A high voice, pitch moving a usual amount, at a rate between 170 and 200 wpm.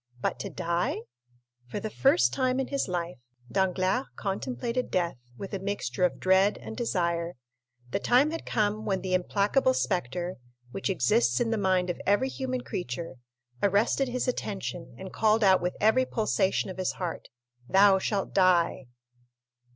No: high, 195 Hz; average, 3.8 semitones; average, 160 wpm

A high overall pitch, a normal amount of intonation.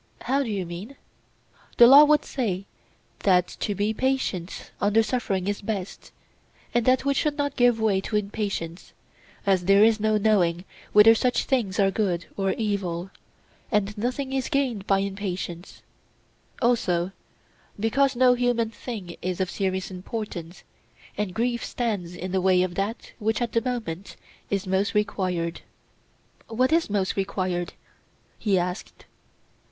Yes: high, 205 Hz; average, 4.2 semitones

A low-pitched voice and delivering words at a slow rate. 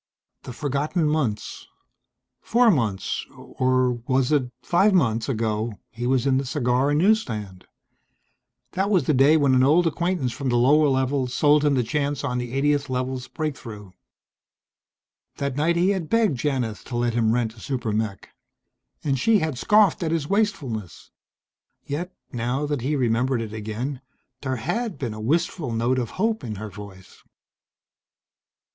No: low, 130 Hz; average, 165 wpm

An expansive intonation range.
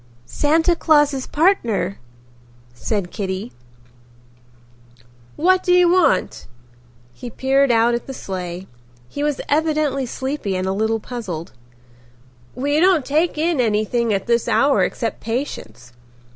Yes: wide, 6.3 semitones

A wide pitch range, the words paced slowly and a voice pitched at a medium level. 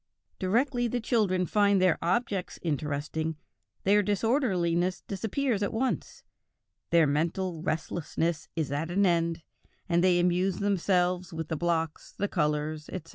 No: average, 3.8 semitones; slow, 130 wpm; medium, 180 Hz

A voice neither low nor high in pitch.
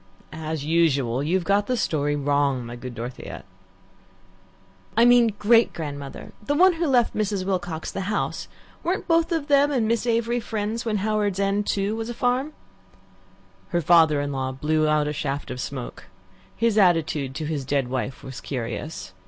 Yes: medium, 175 Hz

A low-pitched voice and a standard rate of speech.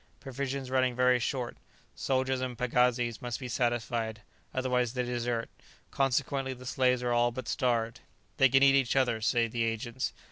Yes: low, 125 Hz; average, 165 wpm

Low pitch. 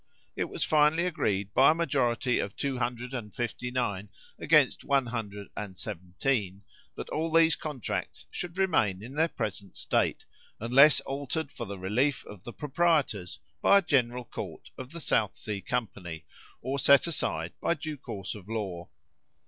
Yes: low, 125 Hz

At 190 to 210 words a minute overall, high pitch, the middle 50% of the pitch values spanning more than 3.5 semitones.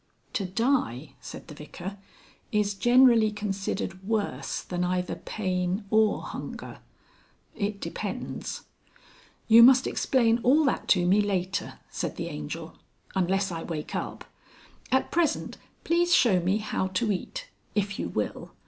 No: slow, 135 wpm; high, 200 Hz; average, 4.2 semitones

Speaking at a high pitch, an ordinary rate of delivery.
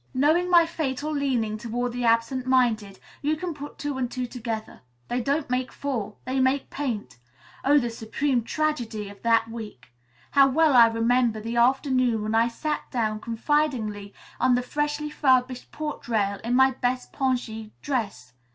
Yes: very high, 250 Hz; average, 165 wpm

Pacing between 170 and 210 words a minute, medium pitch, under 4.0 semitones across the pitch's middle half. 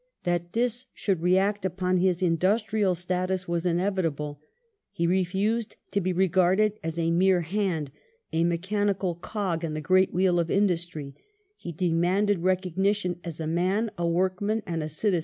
No: average, 155 wpm; medium, 180 Hz; narrow, 2.6 semitones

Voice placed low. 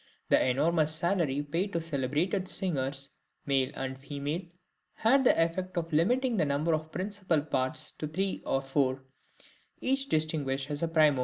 No: medium, 155 Hz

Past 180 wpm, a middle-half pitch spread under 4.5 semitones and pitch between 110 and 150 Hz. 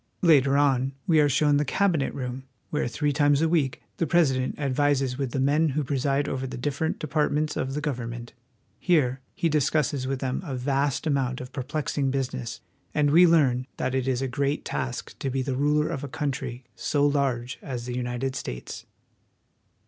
Yes: average, 190 wpm; narrow, 2.4 semitones; low, 135 Hz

